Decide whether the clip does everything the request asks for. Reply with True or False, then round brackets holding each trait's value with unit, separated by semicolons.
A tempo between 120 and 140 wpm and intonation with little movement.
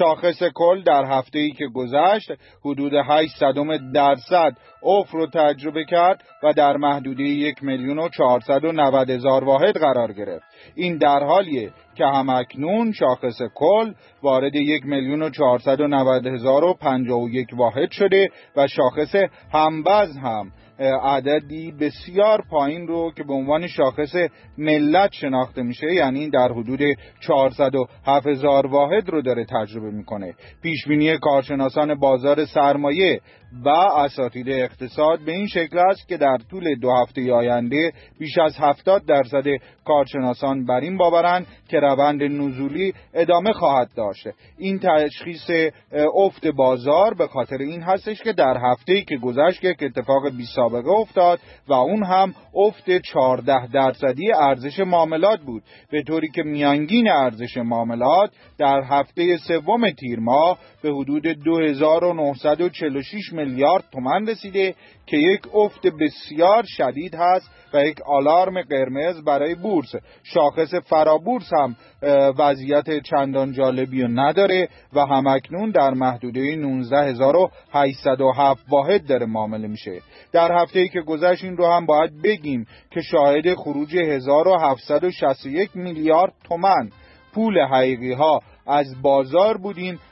False (125 wpm; 4.4 semitones)